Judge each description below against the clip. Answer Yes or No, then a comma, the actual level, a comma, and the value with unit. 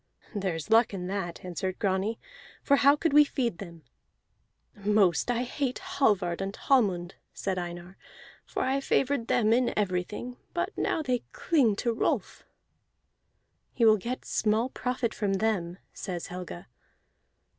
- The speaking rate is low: No, average, 145 wpm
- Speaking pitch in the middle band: No, high, 215 Hz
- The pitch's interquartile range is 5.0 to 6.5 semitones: Yes, average, 5.3 semitones